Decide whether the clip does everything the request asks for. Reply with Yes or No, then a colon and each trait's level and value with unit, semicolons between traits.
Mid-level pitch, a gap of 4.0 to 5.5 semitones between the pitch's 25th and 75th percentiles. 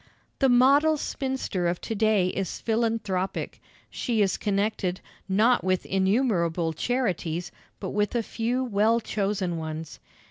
No: high, 205 Hz; average, 4.3 semitones